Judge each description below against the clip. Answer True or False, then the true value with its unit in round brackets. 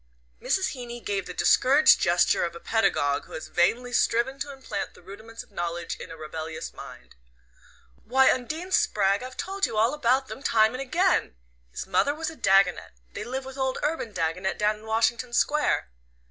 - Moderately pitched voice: False (230 Hz)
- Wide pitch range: True (5.8 semitones)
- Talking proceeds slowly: False (185 wpm)